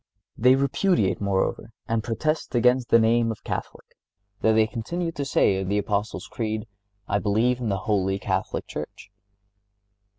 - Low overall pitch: Yes, low, 110 Hz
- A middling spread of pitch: Yes, average, 3.3 semitones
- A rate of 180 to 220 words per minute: No, average, 155 wpm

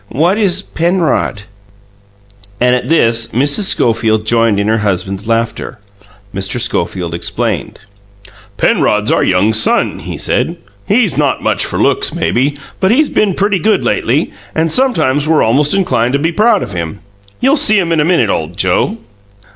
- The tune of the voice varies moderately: No, wide, 9.0 semitones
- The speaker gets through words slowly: No, average, 160 wpm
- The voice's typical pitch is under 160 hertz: Yes, low, 135 Hz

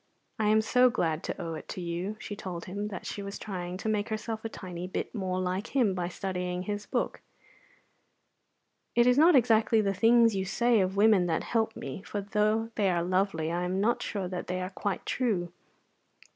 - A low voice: No, high, 200 Hz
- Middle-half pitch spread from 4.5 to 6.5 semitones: No, average, 3.3 semitones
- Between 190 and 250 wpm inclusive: Yes, fast, 205 wpm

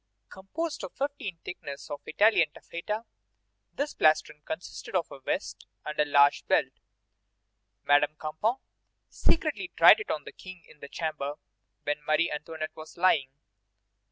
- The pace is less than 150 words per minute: Yes, average, 140 wpm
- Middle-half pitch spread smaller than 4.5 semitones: No, average, 5.2 semitones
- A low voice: No, medium, 160 Hz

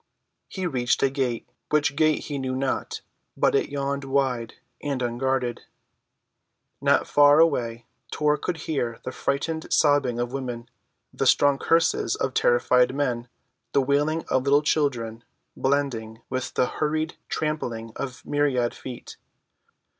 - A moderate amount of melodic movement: Yes, average, 3.0 semitones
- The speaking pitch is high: No, low, 135 Hz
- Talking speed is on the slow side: Yes, slow, 130 wpm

